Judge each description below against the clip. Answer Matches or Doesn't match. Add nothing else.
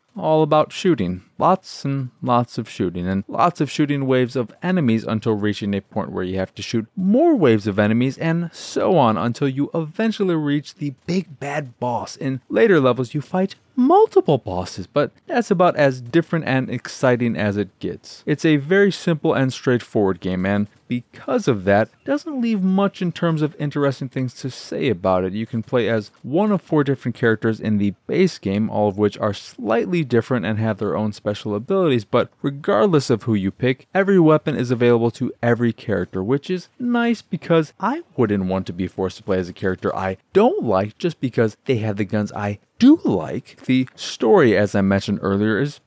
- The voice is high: Doesn't match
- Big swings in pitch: Matches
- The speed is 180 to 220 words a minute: Matches